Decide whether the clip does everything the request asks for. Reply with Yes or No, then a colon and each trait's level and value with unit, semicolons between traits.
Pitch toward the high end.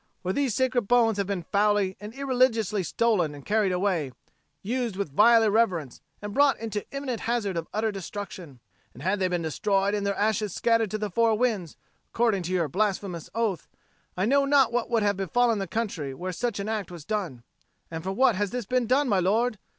Yes: high, 205 Hz